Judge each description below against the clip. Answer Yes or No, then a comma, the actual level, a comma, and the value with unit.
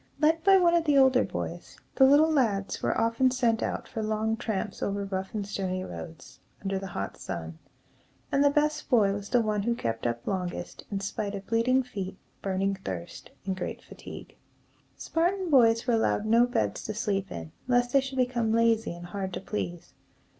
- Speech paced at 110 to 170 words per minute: No, average, 190 wpm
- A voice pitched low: No, high, 220 Hz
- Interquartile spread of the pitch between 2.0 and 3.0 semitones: No, average, 4.7 semitones